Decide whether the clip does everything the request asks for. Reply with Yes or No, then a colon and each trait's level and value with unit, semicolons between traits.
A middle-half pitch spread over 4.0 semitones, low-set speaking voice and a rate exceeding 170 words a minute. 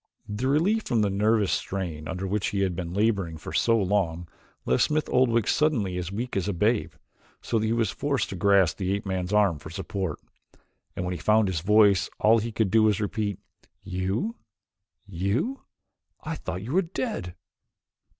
No: average, 3.7 semitones; low, 100 Hz; average, 190 wpm